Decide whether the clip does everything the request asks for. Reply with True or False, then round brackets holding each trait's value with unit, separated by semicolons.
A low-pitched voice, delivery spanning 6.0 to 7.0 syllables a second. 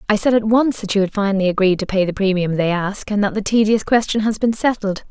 False (205 Hz; 6.1 syllables/s)